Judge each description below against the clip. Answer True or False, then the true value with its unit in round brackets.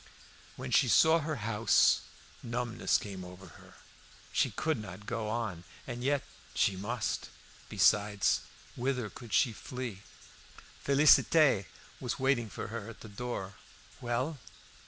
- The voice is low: True (115 Hz)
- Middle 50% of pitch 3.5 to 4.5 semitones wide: True (3.9 semitones)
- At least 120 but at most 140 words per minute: True (135 wpm)